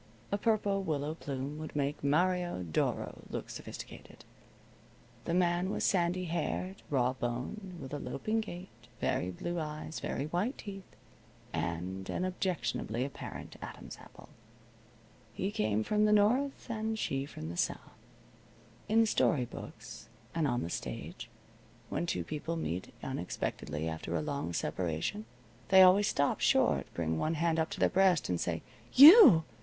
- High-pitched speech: No, medium, 160 Hz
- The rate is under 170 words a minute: Yes, average, 150 wpm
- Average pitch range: No, wide, 7.7 semitones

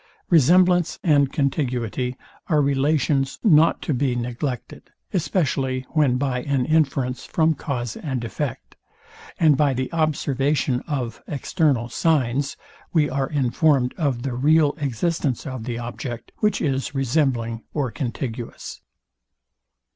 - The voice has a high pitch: No, low, 135 Hz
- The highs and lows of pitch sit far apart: No, average, 3.5 semitones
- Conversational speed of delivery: No, slow, 120 wpm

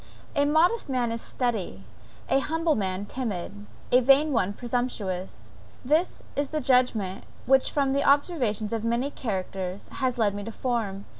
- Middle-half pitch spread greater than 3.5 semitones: Yes, average, 5.2 semitones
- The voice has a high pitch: Yes, high, 245 Hz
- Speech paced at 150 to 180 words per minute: Yes, average, 155 wpm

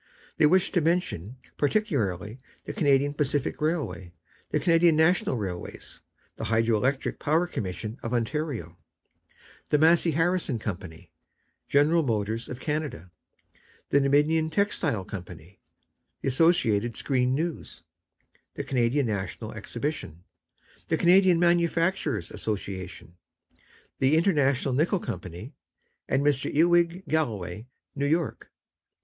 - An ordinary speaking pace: No, slow, 110 wpm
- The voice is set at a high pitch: No, medium, 140 Hz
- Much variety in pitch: Yes, wide, 7.0 semitones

